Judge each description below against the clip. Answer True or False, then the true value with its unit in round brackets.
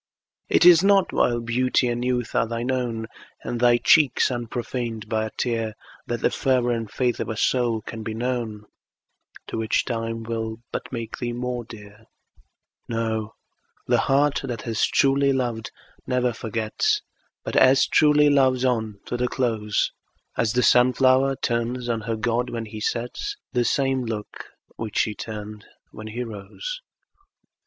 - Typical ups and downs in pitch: False (2.2 semitones)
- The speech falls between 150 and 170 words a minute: True (160 wpm)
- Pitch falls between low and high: False (120 Hz)